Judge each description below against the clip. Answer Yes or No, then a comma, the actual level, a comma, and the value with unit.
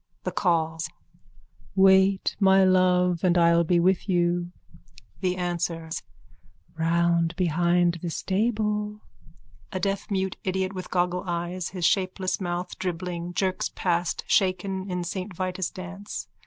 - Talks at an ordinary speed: No, slow, 125 wpm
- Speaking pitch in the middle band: Yes, medium, 180 Hz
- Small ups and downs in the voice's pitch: Yes, narrow, 1.6 semitones